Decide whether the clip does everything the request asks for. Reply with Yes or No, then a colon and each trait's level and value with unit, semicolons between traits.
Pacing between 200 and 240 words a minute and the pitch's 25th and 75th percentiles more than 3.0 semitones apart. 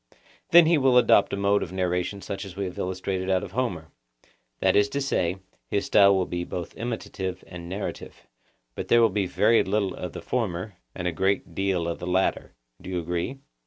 No: fast, 205 wpm; average, 2.7 semitones